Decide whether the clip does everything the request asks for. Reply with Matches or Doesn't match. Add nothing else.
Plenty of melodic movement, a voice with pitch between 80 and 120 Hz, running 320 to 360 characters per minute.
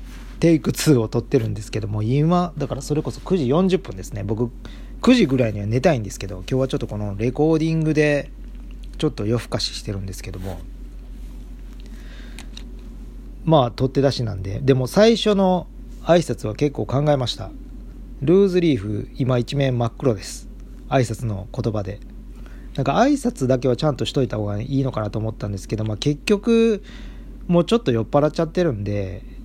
Doesn't match